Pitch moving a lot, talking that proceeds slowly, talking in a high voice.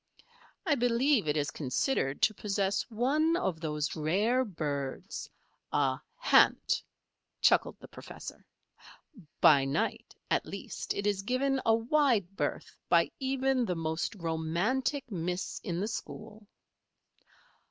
Yes: wide, 7.9 semitones; slow, 120 wpm; high, 205 Hz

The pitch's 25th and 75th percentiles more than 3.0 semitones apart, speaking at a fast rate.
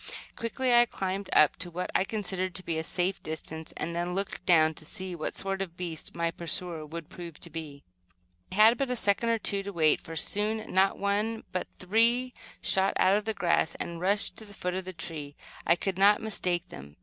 Yes: average, 3.4 semitones; fast, 220 wpm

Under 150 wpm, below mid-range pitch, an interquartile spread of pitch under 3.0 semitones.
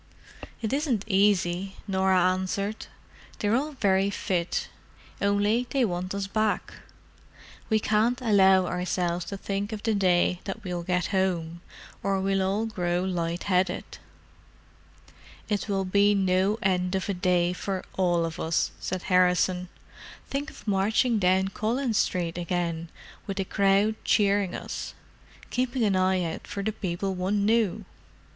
No: average, 140 wpm; high, 190 Hz; narrow, 2.4 semitones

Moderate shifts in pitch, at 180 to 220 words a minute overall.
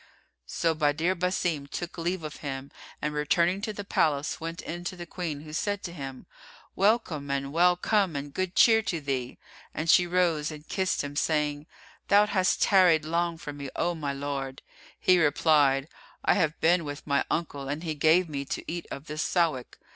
Yes: average, 3.6 semitones; average, 190 wpm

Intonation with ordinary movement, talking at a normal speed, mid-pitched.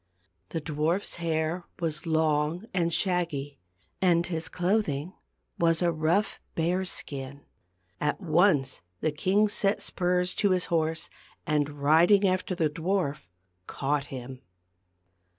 No: average, 3.3 semitones; slow, 120 wpm; medium, 165 Hz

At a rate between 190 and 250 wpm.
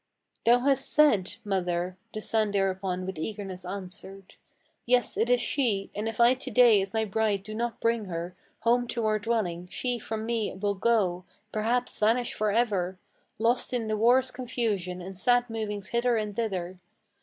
No: average, 175 wpm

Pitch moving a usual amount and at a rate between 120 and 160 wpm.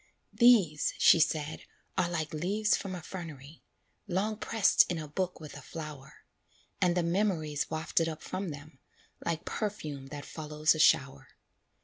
Yes: average, 3.6 semitones; average, 150 wpm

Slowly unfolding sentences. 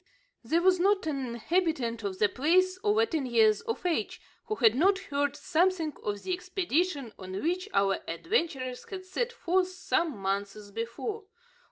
No: average, 160 wpm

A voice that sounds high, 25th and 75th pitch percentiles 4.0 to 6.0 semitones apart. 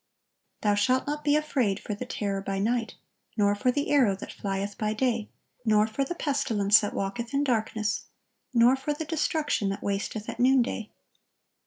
Yes: high, 225 Hz; average, 4.8 semitones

